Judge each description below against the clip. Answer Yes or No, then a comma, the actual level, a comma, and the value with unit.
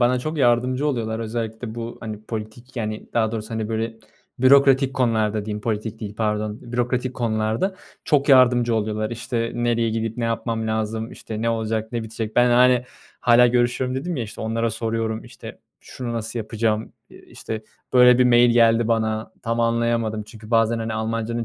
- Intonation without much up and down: Yes, narrow, 1.7 semitones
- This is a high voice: No, low, 115 Hz